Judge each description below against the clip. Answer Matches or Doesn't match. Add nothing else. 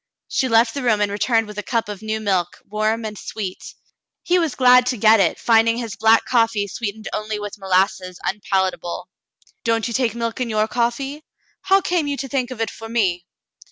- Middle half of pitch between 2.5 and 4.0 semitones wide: Matches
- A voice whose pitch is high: Matches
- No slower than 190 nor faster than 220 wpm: Matches